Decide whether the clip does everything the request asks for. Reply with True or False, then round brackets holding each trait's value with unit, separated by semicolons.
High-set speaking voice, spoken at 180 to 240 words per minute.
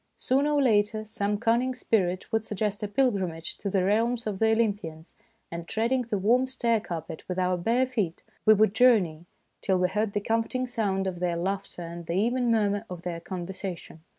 True (205 Hz; 190 wpm)